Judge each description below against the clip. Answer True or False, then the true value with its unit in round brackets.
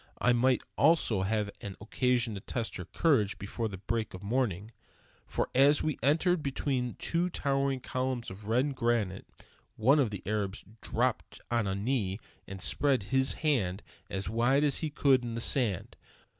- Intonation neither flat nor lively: True (4.9 semitones)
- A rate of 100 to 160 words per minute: False (170 wpm)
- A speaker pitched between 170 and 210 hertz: False (120 Hz)